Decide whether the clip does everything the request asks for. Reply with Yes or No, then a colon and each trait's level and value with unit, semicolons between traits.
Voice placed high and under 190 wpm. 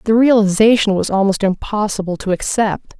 Yes: high, 205 Hz; average, 140 wpm